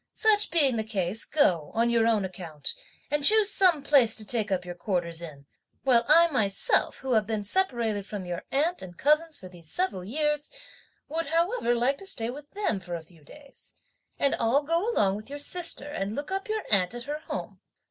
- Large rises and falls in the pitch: Yes, wide, 7.7 semitones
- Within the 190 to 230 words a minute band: Yes, fast, 205 wpm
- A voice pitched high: Yes, high, 240 Hz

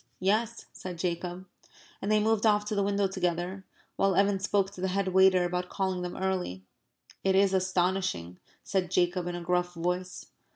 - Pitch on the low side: No, medium, 185 Hz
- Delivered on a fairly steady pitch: Yes, narrow, 1.7 semitones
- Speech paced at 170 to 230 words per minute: Yes, average, 175 wpm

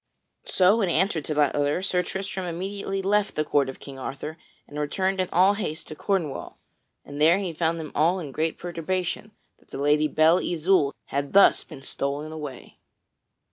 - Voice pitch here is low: No, medium, 165 Hz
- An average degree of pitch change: Yes, average, 4.2 semitones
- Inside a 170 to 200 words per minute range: Yes, average, 180 wpm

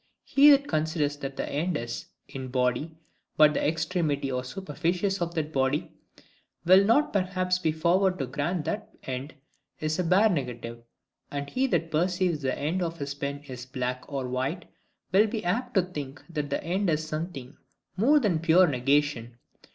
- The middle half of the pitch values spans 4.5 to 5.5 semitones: Yes, average, 4.8 semitones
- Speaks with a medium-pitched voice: Yes, medium, 155 Hz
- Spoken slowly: No, average, 180 wpm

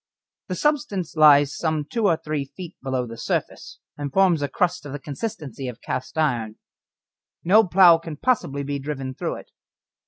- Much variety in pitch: No, average, 4.6 semitones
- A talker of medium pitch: Yes, medium, 150 Hz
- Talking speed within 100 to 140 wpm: No, average, 175 wpm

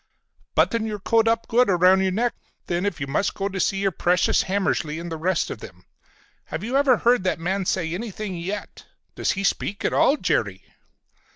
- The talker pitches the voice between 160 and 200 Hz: Yes, high, 190 Hz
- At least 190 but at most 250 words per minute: Yes, average, 200 wpm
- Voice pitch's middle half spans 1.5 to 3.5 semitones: No, average, 3.9 semitones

